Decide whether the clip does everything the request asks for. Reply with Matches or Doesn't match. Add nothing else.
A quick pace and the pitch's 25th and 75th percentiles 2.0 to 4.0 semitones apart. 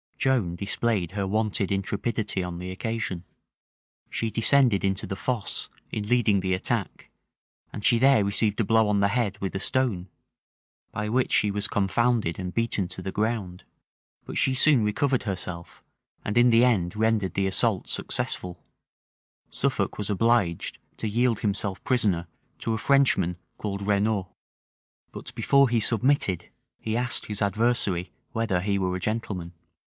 Doesn't match